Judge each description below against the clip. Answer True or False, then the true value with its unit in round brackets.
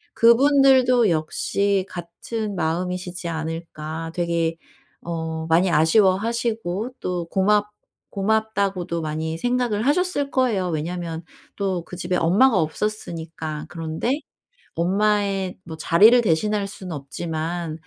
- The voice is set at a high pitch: False (180 Hz)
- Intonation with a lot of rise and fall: False (4.6 semitones)